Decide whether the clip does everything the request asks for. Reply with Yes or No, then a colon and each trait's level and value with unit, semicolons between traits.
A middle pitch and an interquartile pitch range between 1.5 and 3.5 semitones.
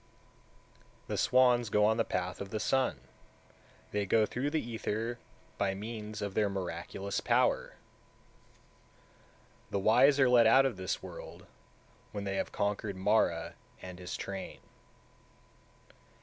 No: low, 105 Hz; average, 3.2 semitones